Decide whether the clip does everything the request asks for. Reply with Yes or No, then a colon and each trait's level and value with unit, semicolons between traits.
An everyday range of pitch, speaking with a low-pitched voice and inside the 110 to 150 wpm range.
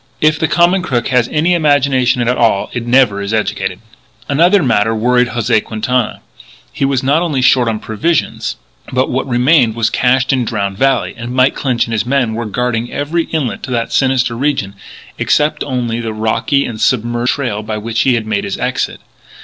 No: average, 3.4 semitones; low, 125 Hz; average, 190 wpm